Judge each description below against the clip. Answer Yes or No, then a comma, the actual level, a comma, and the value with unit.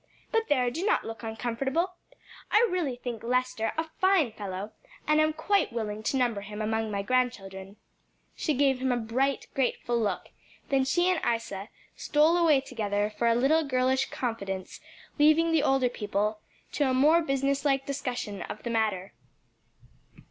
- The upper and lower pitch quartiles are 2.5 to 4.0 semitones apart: No, average, 4.9 semitones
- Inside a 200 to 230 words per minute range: No, average, 165 wpm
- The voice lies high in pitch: Yes, very high, 255 Hz